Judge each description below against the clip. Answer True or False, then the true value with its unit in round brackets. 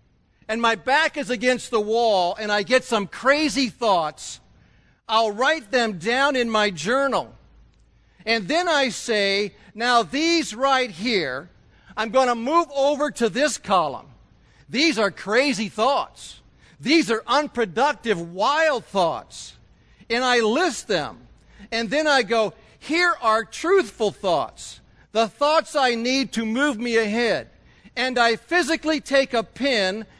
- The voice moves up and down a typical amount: True (4.3 semitones)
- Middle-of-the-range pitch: False (240 Hz)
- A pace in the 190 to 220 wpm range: False (140 wpm)